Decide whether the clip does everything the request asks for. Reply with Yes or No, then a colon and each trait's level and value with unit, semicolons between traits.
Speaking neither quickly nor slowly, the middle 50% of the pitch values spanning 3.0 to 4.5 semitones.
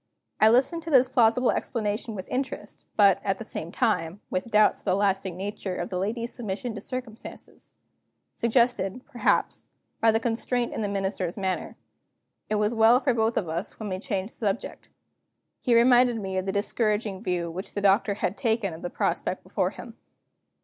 Yes: average, 185 wpm; average, 3.6 semitones